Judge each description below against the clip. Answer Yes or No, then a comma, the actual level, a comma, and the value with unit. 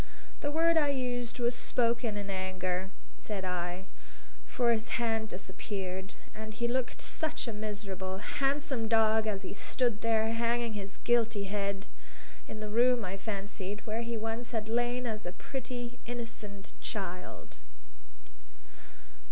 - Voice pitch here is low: No, high, 220 Hz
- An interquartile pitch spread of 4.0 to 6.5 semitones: No, average, 3.3 semitones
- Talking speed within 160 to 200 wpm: No, average, 140 wpm